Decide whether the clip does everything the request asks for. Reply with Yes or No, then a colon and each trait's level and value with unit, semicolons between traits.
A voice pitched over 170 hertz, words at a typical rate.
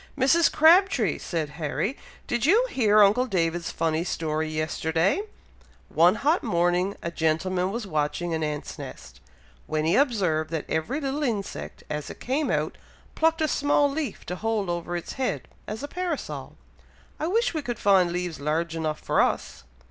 Yes: medium, 185 Hz; average, 165 wpm